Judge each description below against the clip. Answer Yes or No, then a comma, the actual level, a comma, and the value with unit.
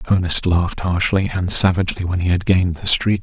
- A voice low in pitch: Yes, very low, 90 Hz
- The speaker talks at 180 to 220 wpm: Yes, fast, 205 wpm